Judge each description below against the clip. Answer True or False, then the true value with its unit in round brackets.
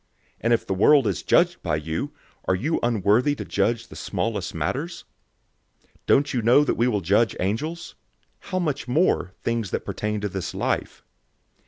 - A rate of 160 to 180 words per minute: True (175 wpm)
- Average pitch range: False (6.5 semitones)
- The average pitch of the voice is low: True (115 Hz)